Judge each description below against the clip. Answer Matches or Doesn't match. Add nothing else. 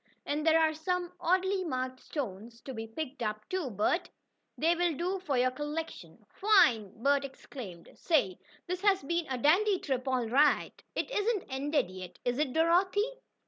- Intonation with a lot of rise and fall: Matches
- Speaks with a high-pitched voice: Matches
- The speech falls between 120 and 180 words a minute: Matches